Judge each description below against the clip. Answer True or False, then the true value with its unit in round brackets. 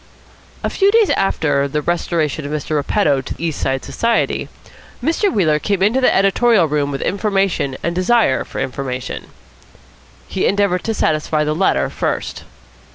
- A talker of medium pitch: True (170 Hz)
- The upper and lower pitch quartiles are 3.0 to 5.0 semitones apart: False (5.6 semitones)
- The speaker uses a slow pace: False (155 wpm)